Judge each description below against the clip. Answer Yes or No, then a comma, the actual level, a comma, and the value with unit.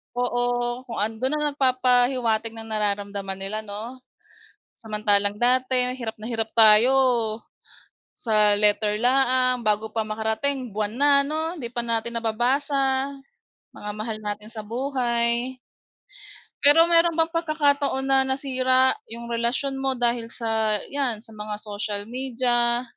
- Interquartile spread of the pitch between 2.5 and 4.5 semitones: Yes, average, 3.3 semitones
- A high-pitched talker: Yes, high, 235 Hz